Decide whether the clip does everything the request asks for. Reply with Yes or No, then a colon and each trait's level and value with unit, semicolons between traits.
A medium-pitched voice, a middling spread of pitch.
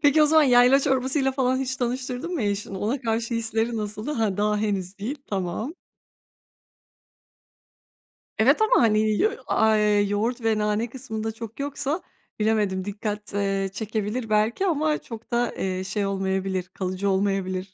No: high, 220 Hz; average, 3.9 semitones